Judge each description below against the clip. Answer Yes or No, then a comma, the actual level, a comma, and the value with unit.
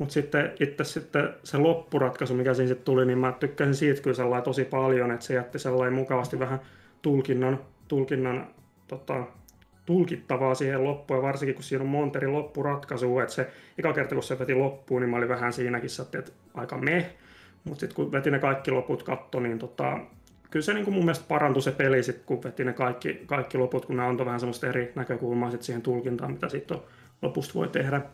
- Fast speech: Yes, fast, 195 wpm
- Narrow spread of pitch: Yes, narrow, 2.1 semitones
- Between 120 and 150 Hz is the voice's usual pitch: Yes, low, 130 Hz